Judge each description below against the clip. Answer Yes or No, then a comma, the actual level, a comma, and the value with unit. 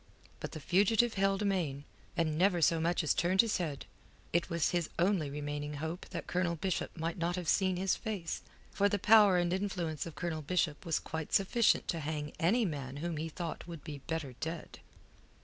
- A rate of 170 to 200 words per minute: Yes, average, 195 wpm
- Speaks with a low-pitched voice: No, medium, 170 Hz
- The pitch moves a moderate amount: Yes, average, 3.3 semitones